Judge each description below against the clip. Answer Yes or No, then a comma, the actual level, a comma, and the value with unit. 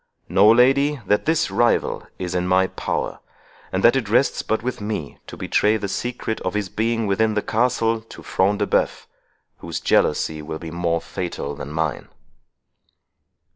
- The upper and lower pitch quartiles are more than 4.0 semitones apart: Yes, average, 4.4 semitones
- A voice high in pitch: No, low, 105 Hz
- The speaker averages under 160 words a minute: No, average, 170 wpm